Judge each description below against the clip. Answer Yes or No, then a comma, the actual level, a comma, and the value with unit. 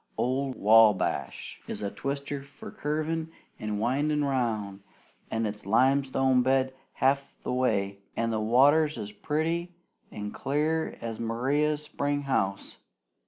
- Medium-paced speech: No, slow, 125 wpm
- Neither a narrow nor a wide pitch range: Yes, average, 4.8 semitones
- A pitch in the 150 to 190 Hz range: No, low, 130 Hz